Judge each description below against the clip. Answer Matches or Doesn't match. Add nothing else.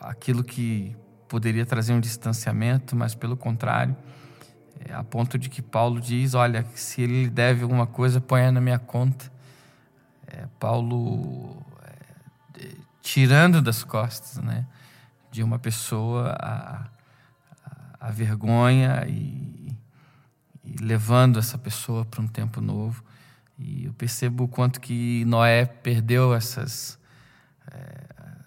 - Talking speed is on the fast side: Doesn't match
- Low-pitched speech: Matches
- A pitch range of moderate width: Doesn't match